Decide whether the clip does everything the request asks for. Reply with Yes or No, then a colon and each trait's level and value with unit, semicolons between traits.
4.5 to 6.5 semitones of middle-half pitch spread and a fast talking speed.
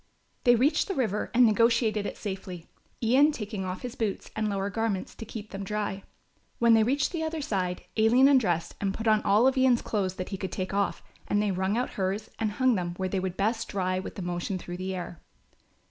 No: average, 3.6 semitones; fast, 225 wpm